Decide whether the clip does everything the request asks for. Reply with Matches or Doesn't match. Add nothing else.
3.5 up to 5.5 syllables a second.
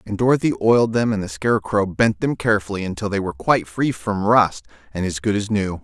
Doesn't match